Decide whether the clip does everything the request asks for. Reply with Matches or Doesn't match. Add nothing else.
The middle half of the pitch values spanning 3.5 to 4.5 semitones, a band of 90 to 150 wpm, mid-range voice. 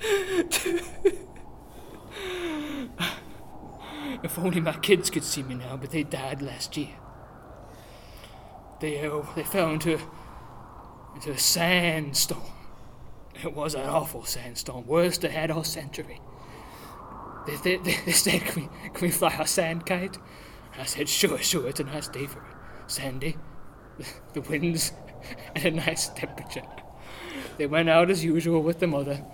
Matches